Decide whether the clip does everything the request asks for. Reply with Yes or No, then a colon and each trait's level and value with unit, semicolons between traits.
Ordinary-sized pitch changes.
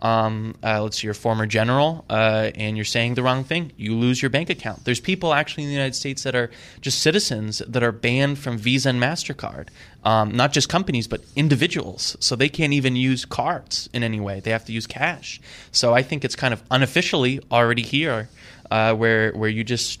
Yes: average, 3.7 semitones